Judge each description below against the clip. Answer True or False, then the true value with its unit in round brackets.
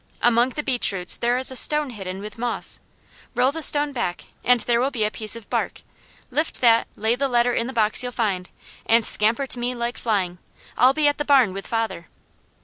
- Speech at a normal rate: False (220 wpm)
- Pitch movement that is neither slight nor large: True (3.3 semitones)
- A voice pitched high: True (240 Hz)